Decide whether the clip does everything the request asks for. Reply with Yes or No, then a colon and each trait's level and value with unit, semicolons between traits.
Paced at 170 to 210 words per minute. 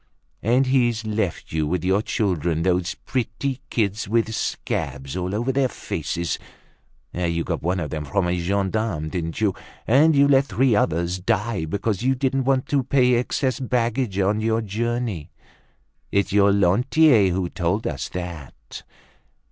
No: average, 155 wpm